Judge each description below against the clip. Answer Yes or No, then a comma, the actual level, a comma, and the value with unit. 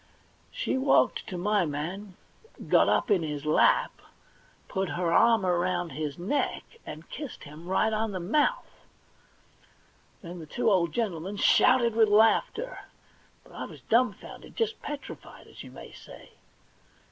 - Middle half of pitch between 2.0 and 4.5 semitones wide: No, average, 5.3 semitones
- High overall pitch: Yes, high, 195 Hz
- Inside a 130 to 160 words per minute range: Yes, average, 145 wpm